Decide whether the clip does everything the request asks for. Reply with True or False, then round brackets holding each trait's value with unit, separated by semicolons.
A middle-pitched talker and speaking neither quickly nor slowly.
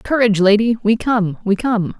False (215 Hz; 180 wpm)